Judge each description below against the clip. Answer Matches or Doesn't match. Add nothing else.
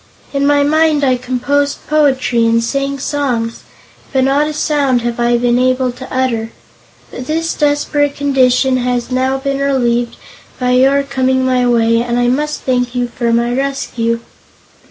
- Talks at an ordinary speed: Matches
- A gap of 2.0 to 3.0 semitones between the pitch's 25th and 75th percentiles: Matches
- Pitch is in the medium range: Doesn't match